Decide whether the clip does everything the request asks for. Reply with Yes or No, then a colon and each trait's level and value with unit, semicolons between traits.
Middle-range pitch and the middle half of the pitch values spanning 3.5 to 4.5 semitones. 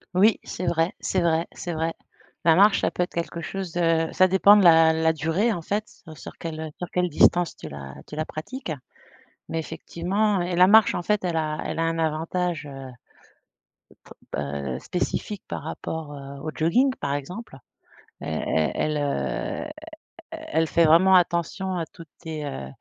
No: medium, 165 Hz; average, 2.8 semitones